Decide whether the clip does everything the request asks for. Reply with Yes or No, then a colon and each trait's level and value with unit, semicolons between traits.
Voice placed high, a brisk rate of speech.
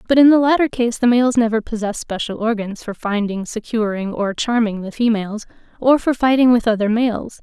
No: high, 225 Hz; average, 195 wpm